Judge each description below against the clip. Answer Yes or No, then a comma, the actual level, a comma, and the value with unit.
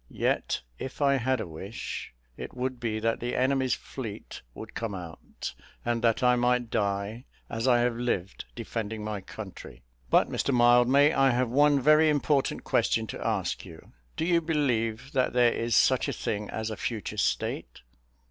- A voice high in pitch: No, low, 120 Hz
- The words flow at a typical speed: Yes, average, 175 wpm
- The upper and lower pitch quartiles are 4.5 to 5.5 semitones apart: No, average, 3.2 semitones